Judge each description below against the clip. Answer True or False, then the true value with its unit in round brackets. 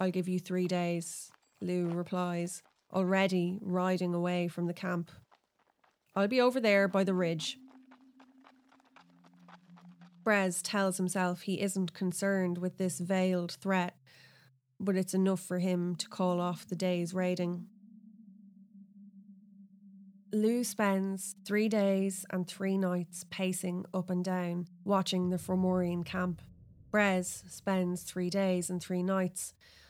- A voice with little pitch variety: True (1.8 semitones)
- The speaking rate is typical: False (125 wpm)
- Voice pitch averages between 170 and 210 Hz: True (185 Hz)